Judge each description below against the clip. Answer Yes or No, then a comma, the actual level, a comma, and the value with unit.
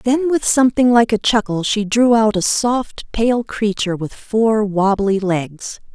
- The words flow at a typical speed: Yes, average, 170 wpm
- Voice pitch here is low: No, high, 220 Hz